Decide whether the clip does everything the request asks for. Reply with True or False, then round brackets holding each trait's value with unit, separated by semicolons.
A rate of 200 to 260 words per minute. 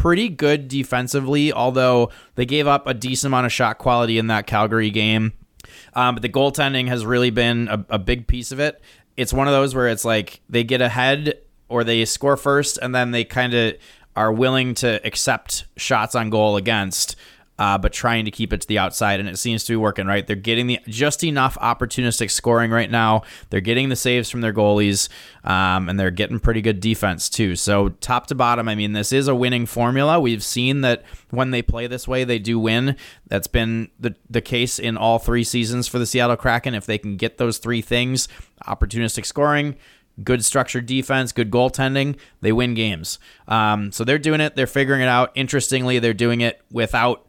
True (205 wpm)